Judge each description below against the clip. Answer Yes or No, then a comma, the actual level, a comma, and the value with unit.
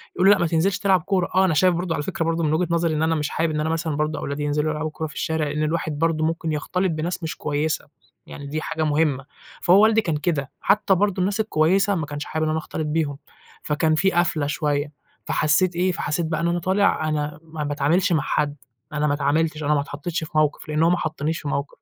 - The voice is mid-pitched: Yes, medium, 160 Hz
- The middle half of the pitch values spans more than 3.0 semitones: No, narrow, 2.5 semitones